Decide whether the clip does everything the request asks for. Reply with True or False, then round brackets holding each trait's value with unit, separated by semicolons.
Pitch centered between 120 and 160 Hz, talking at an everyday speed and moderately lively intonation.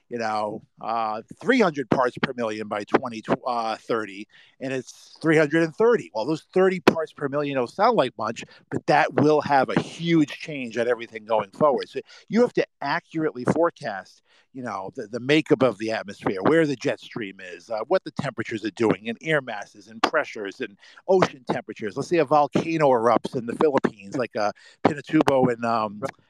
False (135 Hz; 180 wpm; 5.9 semitones)